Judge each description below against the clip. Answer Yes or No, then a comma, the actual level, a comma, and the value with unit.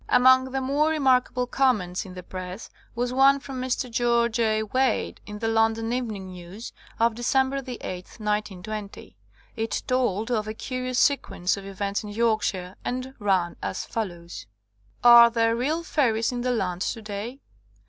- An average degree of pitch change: Yes, average, 3.8 semitones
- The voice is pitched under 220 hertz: No, high, 230 Hz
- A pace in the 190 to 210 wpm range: No, average, 160 wpm